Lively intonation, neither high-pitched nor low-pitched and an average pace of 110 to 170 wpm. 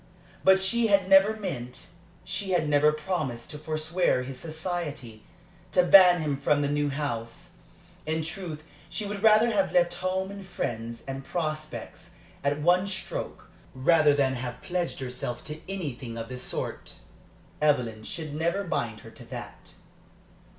Yes: wide, 5.8 semitones; medium, 155 Hz; average, 150 wpm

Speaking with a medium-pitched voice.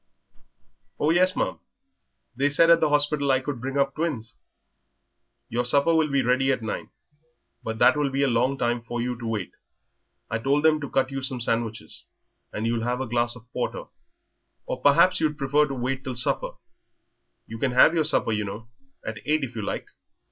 No: low, 130 Hz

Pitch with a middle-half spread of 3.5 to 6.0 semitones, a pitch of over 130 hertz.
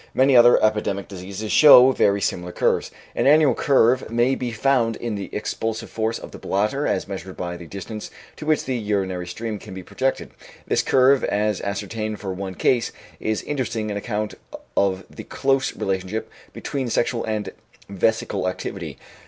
No: average, 3.9 semitones; low, 110 Hz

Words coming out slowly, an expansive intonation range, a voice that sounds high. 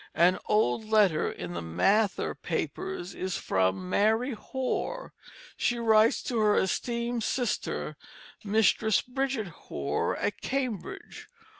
No: slow, 115 wpm; average, 5.0 semitones; high, 215 Hz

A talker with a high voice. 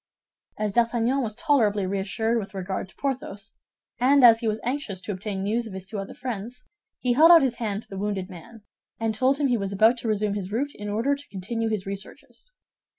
Yes: high, 220 Hz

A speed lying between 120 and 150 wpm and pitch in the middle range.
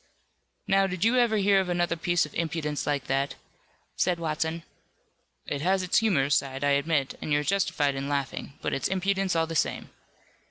No: average, 185 wpm; medium, 165 Hz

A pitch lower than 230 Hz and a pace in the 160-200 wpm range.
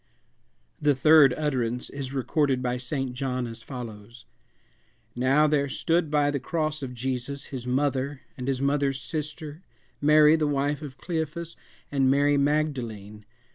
No: medium, 140 Hz; average, 140 wpm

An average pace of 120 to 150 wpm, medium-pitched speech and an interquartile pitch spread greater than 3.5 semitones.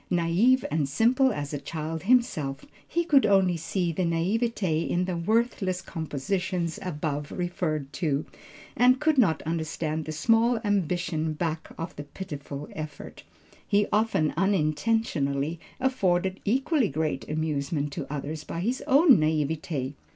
Yes: slow, 135 wpm; medium, 170 Hz; average, 5.3 semitones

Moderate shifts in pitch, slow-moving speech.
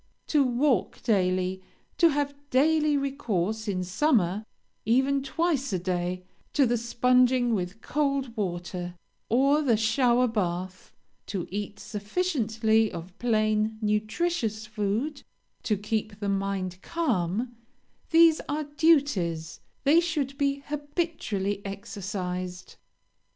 No: wide, 6.2 semitones; slow, 110 wpm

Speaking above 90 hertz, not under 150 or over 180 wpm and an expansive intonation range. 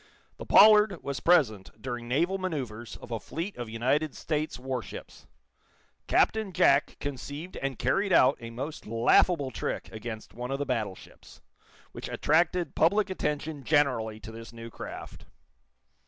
No: low, 135 Hz; average, 140 wpm; wide, 5.7 semitones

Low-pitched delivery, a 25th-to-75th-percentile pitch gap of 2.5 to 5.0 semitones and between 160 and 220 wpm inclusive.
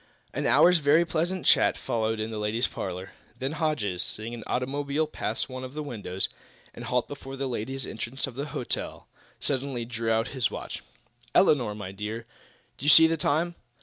Yes: low, 130 Hz; average, 4.5 semitones; average, 180 wpm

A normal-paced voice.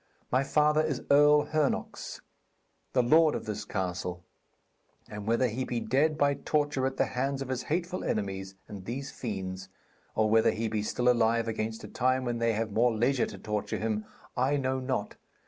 Yes: average, 180 wpm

